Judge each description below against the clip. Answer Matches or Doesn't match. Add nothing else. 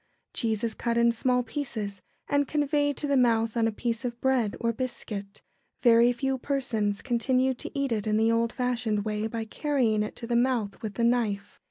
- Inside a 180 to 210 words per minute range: Matches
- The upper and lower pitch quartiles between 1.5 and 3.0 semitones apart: Matches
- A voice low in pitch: Doesn't match